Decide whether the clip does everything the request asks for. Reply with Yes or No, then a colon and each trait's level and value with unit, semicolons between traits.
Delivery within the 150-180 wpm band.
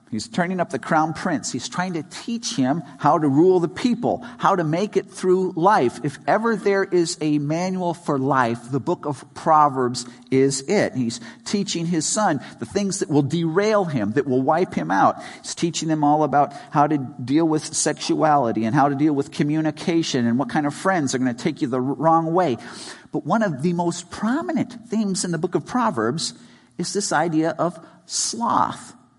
No: average, 200 wpm